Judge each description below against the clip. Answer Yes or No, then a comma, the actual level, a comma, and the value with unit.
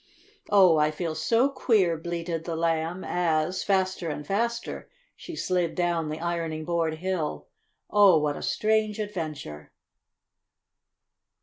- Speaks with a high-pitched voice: No, medium, 170 Hz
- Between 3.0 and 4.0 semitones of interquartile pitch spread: Yes, average, 3.3 semitones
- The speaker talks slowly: Yes, slow, 125 wpm